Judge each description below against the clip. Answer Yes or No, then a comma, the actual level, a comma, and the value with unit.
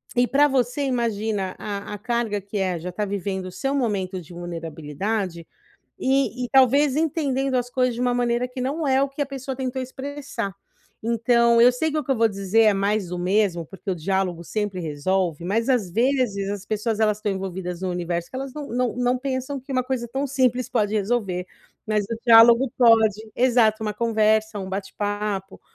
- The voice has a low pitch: No, high, 225 Hz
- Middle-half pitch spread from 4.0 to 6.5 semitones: Yes, average, 4.6 semitones